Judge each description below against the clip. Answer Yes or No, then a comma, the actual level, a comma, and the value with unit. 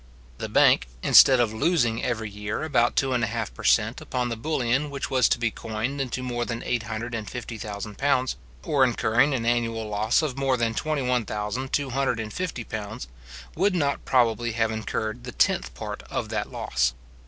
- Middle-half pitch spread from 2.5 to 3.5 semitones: Yes, average, 3.1 semitones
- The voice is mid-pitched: No, low, 120 Hz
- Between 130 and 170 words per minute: No, average, 180 wpm